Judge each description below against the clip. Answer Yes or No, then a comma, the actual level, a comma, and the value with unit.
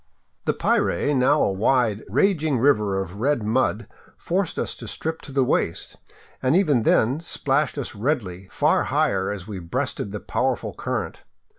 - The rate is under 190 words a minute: Yes, average, 160 wpm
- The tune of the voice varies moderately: No, wide, 6.2 semitones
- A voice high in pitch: No, low, 125 Hz